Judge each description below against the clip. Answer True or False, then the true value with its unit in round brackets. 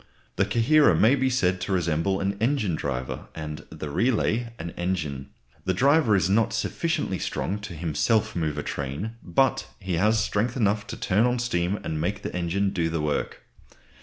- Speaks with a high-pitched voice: False (95 Hz)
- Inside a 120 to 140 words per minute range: False (180 wpm)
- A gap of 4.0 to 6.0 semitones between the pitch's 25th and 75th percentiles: True (5.3 semitones)